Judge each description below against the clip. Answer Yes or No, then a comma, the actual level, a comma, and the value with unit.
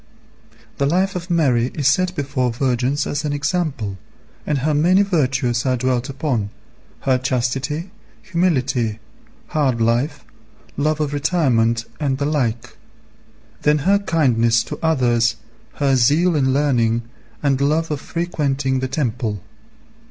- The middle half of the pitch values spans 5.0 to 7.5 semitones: No, average, 3.8 semitones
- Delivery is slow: Yes, slow, 130 wpm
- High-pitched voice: No, medium, 140 Hz